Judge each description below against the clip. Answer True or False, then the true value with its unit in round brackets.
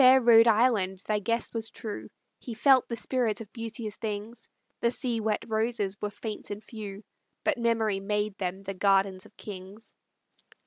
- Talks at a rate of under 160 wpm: False (175 wpm)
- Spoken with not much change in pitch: True (2.3 semitones)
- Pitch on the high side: True (220 Hz)